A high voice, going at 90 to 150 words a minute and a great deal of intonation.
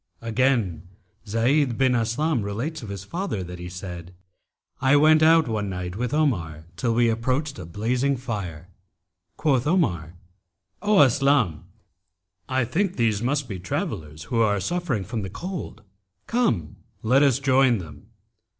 No: low, 115 Hz; average, 145 wpm; wide, 6.8 semitones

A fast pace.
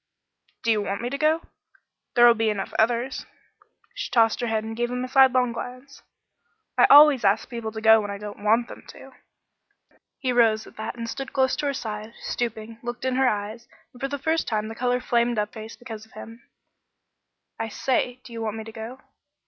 Yes: fast, 220 wpm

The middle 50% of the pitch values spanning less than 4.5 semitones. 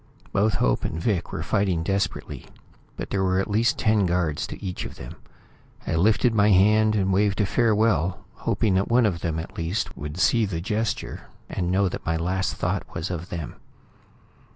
Yes: average, 3.6 semitones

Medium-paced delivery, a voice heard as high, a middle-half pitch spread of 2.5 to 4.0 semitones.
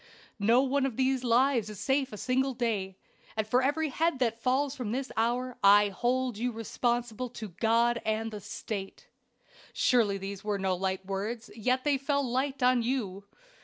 Yes: average, 175 wpm; high, 240 Hz; average, 3.6 semitones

